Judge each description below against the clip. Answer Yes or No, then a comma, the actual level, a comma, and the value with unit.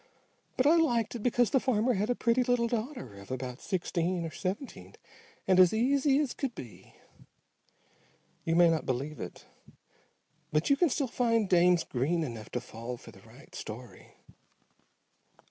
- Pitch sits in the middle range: No, high, 200 Hz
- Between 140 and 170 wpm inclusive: Yes, average, 160 wpm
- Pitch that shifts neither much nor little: No, wide, 8.0 semitones